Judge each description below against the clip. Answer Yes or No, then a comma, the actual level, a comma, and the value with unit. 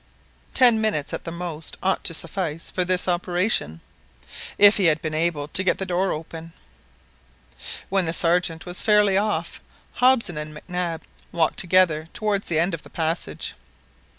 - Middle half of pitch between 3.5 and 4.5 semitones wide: No, average, 2.9 semitones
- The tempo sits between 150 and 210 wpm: Yes, average, 165 wpm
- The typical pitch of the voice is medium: Yes, medium, 175 Hz